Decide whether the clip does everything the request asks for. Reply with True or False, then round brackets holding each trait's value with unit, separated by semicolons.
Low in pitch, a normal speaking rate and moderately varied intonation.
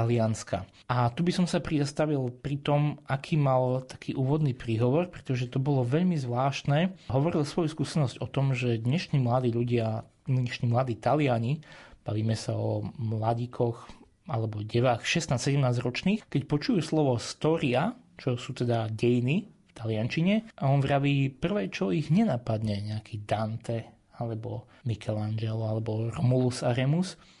True (130 Hz; 135 wpm; 4.1 semitones)